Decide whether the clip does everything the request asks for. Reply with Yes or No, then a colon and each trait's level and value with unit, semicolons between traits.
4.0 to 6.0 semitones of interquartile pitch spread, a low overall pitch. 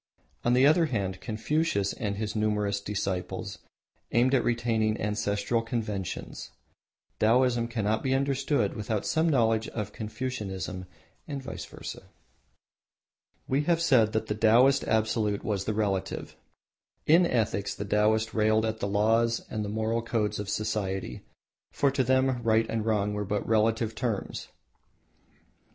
No: average, 2.7 semitones; low, 110 Hz